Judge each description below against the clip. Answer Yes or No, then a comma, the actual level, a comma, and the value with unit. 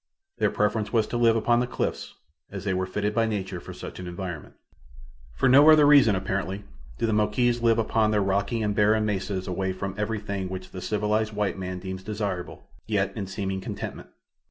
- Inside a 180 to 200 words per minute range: Yes, average, 195 wpm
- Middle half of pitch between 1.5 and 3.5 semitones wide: Yes, average, 2.7 semitones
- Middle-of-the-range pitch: No, low, 105 Hz